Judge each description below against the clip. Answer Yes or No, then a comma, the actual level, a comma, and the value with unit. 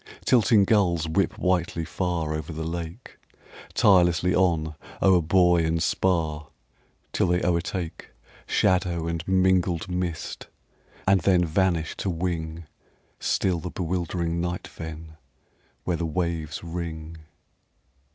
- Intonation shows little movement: Yes, narrow, 2.0 semitones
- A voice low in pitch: Yes, very low, 85 Hz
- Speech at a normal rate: No, slow, 115 wpm